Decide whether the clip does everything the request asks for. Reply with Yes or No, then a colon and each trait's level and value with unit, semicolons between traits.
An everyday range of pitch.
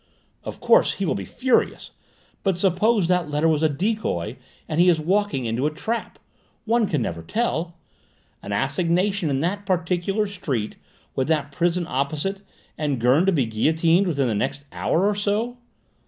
No: wide, 5.8 semitones